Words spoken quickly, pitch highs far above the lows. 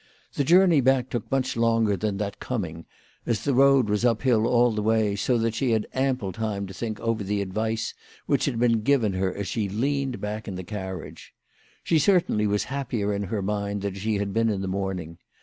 No: fast, 215 wpm; average, 3.5 semitones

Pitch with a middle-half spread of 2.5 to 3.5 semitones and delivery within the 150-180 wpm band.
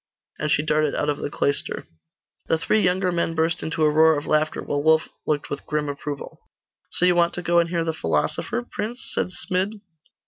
No: average, 2.9 semitones; fast, 205 wpm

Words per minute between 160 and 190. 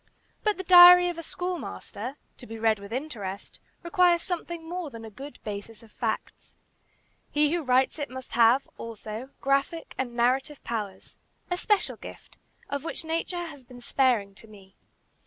Yes: average, 165 wpm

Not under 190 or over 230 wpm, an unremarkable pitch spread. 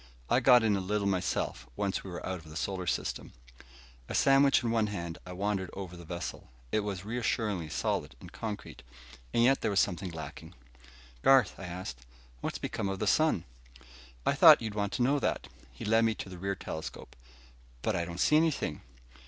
Yes: average, 195 wpm; average, 4.0 semitones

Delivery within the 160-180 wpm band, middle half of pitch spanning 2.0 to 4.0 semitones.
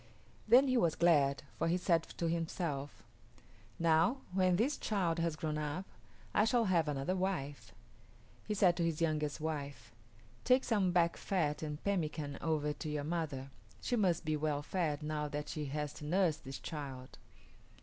Yes: average, 170 wpm; average, 3.5 semitones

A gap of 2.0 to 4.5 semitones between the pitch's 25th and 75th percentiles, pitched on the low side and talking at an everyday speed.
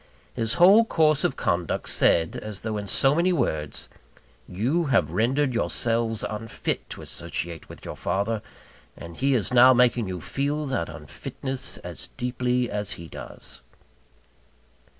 No: average, 5.0 semitones; low, 120 Hz; average, 145 wpm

